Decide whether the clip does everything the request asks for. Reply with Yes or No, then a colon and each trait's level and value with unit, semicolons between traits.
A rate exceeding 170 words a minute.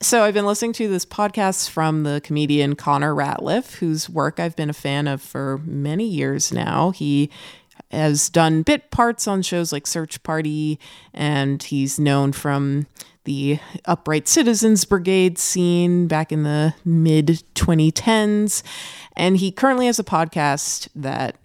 No: average, 150 wpm